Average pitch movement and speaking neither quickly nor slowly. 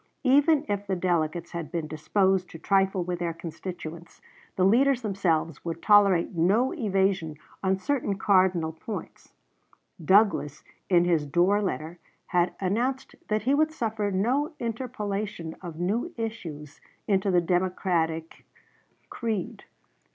No: average, 4.1 semitones; slow, 130 wpm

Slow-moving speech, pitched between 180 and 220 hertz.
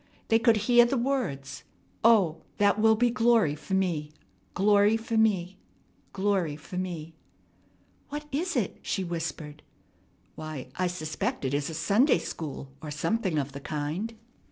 No: average, 155 wpm; medium, 185 Hz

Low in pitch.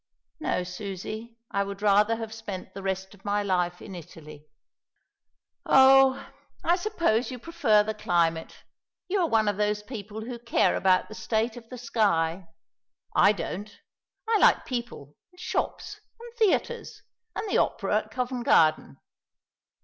No: high, 215 Hz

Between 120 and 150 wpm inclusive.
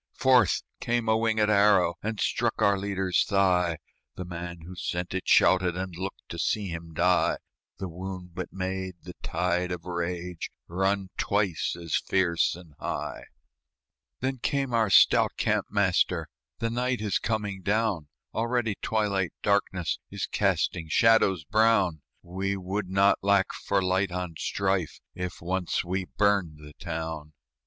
Yes: average, 145 wpm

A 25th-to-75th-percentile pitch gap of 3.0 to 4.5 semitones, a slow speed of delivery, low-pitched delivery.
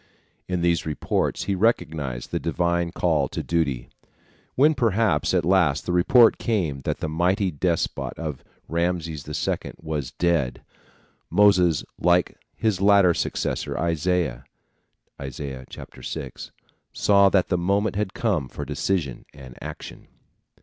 Yes: average, 4.0 semitones; slow, 125 wpm; very low, 85 Hz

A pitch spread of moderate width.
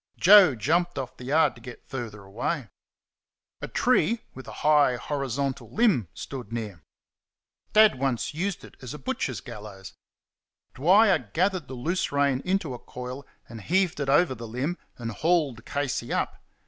No: wide, 5.9 semitones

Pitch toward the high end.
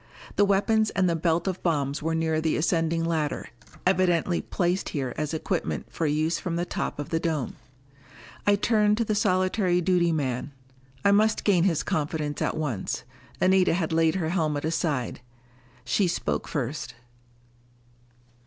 No: medium, 165 Hz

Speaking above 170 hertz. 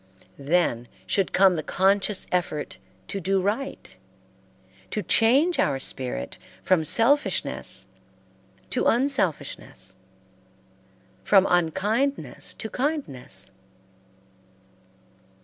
Yes: high, 190 Hz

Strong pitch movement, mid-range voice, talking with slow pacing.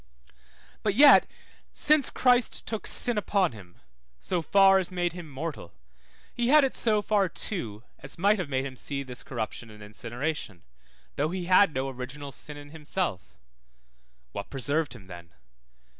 No: wide, 7.5 semitones; medium, 150 Hz; average, 160 wpm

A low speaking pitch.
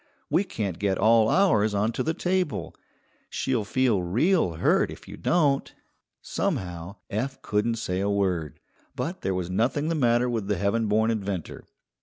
Yes: low, 110 Hz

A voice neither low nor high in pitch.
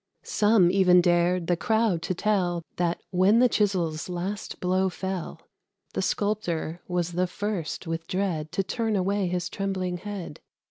Yes: medium, 180 Hz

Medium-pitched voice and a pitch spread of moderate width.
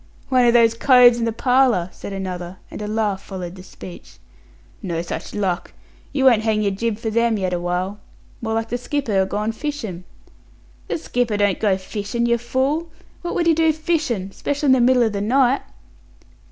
No: high, 225 Hz; average, 4.6 semitones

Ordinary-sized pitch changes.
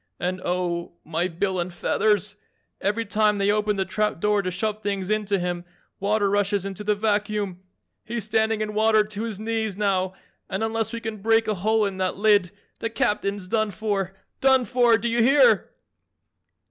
No: narrow, 2.2 semitones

